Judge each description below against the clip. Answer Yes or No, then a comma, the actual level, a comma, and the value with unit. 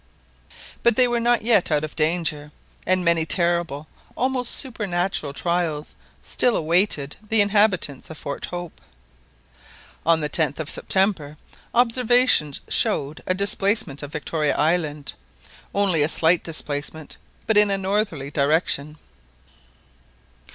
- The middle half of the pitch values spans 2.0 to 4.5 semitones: No, average, 5.1 semitones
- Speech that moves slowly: Yes, slow, 125 wpm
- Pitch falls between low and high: Yes, medium, 170 Hz